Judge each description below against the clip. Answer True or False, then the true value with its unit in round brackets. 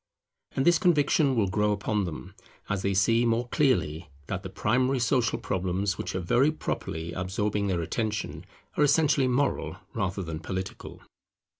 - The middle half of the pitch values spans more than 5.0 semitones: True (5.5 semitones)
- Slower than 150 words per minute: False (155 wpm)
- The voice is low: True (105 Hz)